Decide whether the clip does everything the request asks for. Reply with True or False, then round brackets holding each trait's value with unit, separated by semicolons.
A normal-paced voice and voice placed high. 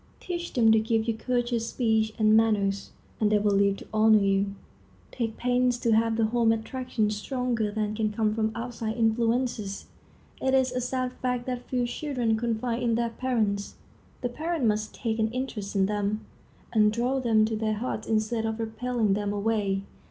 True (180 wpm; 225 Hz)